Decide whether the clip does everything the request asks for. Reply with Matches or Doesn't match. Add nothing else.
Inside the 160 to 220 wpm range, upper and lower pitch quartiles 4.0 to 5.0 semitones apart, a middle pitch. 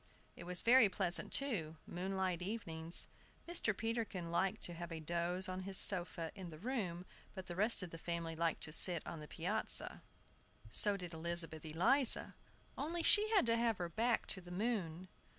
Matches